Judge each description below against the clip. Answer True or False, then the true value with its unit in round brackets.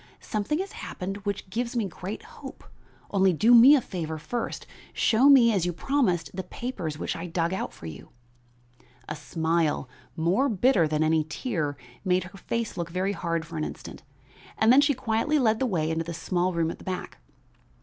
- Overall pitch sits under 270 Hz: True (185 Hz)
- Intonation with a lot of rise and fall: True (6.0 semitones)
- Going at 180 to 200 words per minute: True (190 wpm)